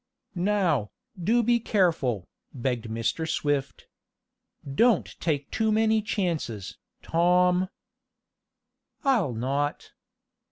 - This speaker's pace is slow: Yes, slow, 85 wpm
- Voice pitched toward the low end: No, medium, 170 Hz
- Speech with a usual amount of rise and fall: No, wide, 7.5 semitones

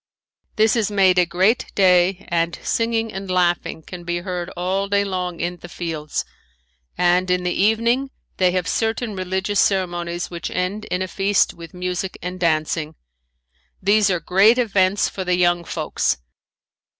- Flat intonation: Yes, narrow, 2.3 semitones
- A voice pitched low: No, medium, 185 Hz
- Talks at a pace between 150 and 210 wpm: Yes, average, 160 wpm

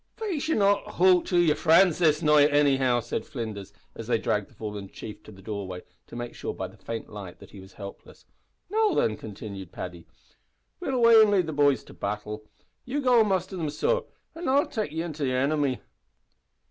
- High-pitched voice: No, medium, 145 Hz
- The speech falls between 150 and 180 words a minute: No, fast, 205 wpm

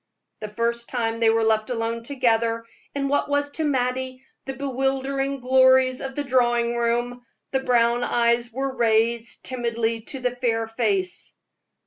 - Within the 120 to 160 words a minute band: Yes, average, 150 wpm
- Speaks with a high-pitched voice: Yes, high, 240 Hz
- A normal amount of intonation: No, narrow, 2.2 semitones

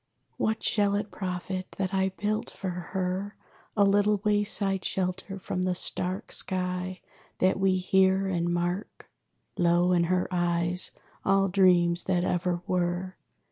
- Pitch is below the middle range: No, medium, 185 Hz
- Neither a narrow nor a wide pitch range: No, narrow, 1.5 semitones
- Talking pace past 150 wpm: No, average, 140 wpm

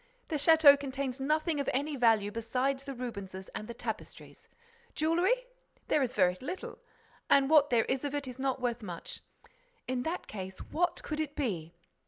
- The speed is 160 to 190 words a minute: Yes, average, 175 wpm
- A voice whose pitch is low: No, very high, 270 Hz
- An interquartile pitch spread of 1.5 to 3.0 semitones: No, average, 4.6 semitones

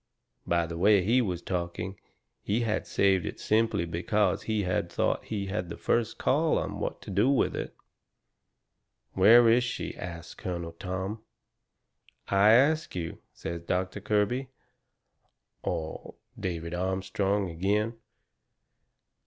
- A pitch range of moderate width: Yes, average, 3.9 semitones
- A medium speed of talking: No, slow, 130 wpm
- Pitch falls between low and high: No, very low, 95 Hz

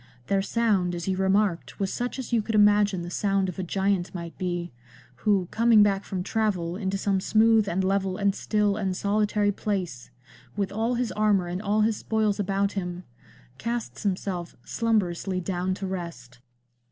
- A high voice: Yes, high, 195 Hz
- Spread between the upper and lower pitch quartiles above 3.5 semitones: No, narrow, 2.5 semitones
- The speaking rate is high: No, average, 175 wpm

